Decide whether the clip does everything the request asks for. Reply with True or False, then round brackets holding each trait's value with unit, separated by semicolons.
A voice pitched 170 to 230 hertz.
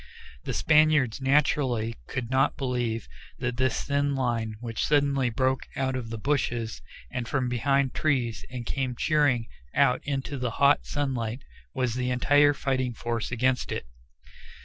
False (130 Hz)